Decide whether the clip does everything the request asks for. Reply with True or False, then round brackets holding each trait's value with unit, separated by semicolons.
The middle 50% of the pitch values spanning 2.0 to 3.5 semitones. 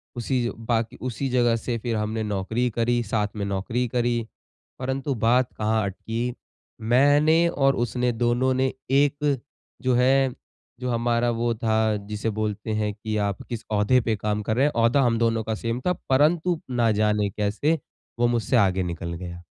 True (2.9 semitones)